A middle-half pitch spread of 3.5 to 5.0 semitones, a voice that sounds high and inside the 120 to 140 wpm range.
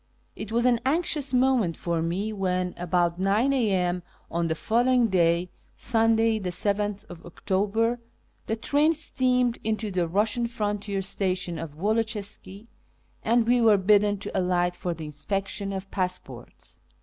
Yes: average, 4.0 semitones; high, 205 Hz; slow, 135 wpm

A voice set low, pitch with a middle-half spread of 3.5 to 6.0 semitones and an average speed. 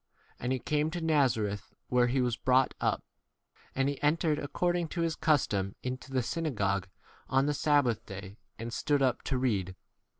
Yes: low, 130 Hz; average, 4.4 semitones; average, 180 wpm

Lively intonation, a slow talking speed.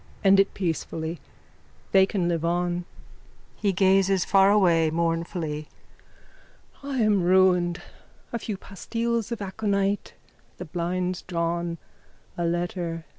No: narrow, 2.6 semitones; slow, 115 wpm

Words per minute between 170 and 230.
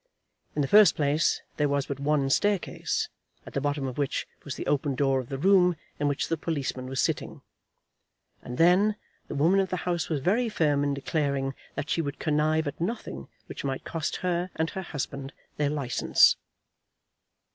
Yes: average, 185 wpm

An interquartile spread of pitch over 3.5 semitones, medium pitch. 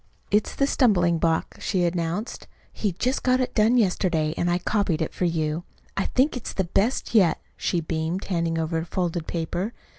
Yes: average, 4.3 semitones; medium, 175 Hz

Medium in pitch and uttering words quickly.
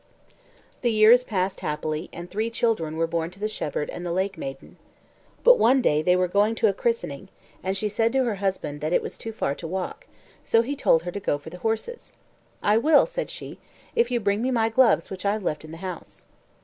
No: high, 200 Hz; fast, 220 wpm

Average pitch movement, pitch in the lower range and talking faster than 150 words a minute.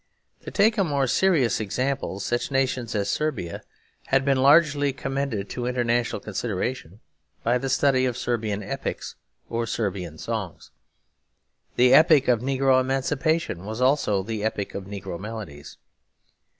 No: average, 4.4 semitones; low, 125 Hz; slow, 135 wpm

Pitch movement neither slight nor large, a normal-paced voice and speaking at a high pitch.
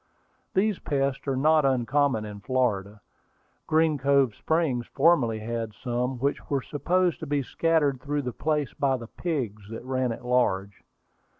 No: average, 3.9 semitones; average, 155 wpm; low, 130 Hz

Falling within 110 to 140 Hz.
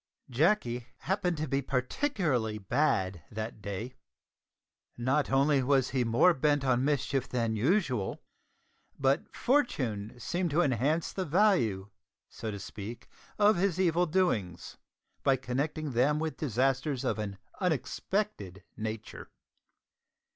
Yes: low, 135 Hz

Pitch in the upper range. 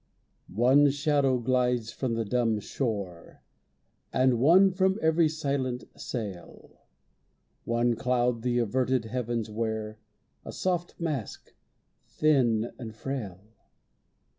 No: low, 125 Hz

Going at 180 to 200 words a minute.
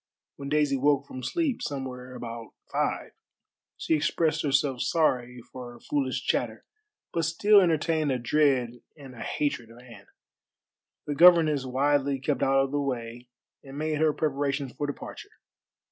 No: average, 150 wpm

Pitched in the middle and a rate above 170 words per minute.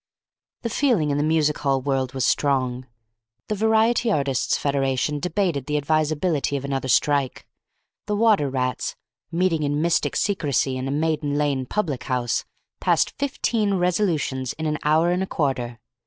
No: medium, 150 Hz; average, 155 wpm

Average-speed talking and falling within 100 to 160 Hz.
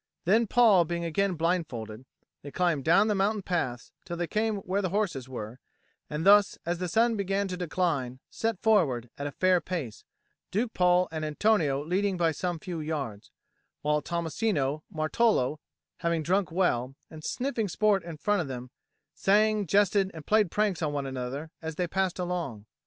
No: average, 175 wpm; medium, 175 Hz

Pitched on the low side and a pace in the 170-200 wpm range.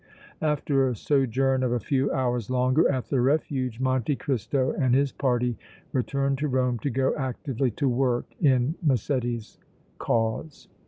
No: low, 130 Hz; average, 150 wpm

